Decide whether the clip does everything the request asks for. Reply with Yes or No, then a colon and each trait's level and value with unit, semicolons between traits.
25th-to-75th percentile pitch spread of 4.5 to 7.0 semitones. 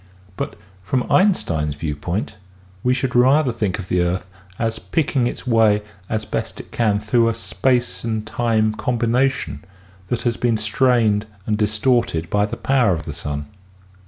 No: average, 3.2 semitones